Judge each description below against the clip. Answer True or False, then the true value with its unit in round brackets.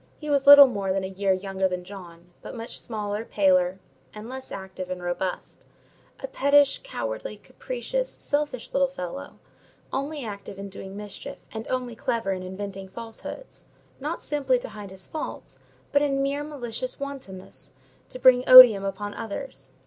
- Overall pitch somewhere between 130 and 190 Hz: False (225 Hz)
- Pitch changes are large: True (6.3 semitones)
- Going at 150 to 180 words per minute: True (160 wpm)